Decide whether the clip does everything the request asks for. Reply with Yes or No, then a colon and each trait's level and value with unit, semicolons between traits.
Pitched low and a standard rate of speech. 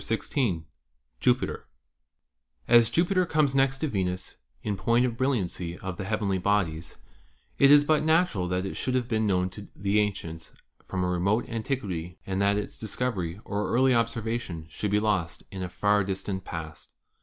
Yes: low, 105 Hz; average, 170 wpm